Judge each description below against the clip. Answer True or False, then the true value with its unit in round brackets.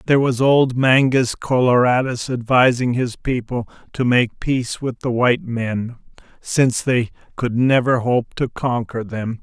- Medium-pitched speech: False (125 Hz)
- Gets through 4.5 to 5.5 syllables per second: False (4.3 syllables/s)